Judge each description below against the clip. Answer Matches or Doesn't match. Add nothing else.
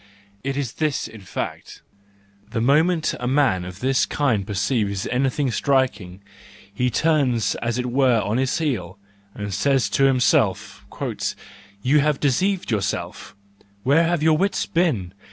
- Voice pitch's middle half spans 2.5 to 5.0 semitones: Doesn't match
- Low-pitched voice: Matches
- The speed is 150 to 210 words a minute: Doesn't match